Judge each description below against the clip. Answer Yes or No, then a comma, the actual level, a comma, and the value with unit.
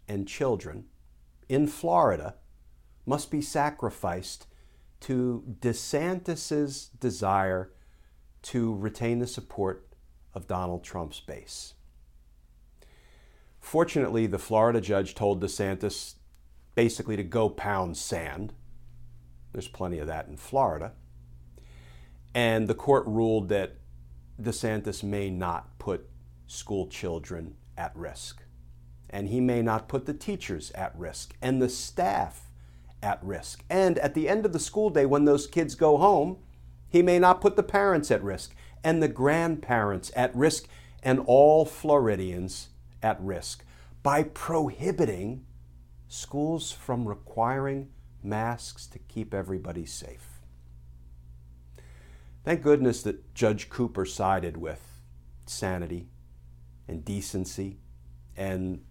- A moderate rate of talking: No, slow, 115 wpm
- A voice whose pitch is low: Yes, very low, 95 Hz